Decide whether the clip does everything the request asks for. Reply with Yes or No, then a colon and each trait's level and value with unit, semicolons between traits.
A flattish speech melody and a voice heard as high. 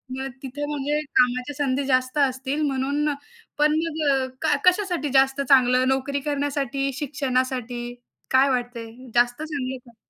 Yes: narrow, 2.2 semitones; very high, 270 Hz